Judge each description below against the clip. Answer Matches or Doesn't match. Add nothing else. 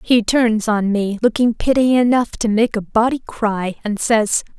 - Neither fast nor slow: Matches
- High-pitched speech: Matches